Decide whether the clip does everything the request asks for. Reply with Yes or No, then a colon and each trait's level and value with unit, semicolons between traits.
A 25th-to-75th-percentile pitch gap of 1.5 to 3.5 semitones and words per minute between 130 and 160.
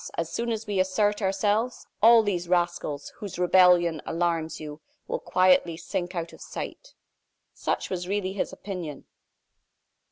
Yes: average, 3.2 semitones; average, 140 wpm